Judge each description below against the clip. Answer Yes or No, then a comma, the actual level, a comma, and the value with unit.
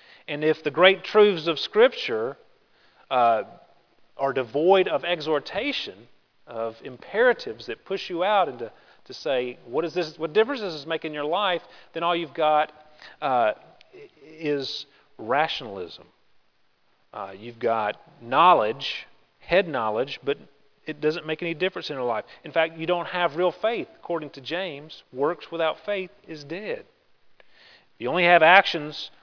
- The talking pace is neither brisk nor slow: Yes, average, 150 wpm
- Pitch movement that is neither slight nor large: Yes, average, 3.5 semitones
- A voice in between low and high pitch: Yes, medium, 165 Hz